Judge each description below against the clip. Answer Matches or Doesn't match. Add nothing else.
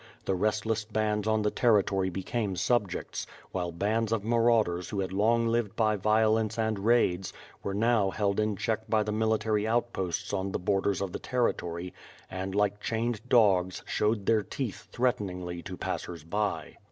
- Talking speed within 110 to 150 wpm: Doesn't match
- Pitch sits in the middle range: Doesn't match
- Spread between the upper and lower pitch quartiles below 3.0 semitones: Matches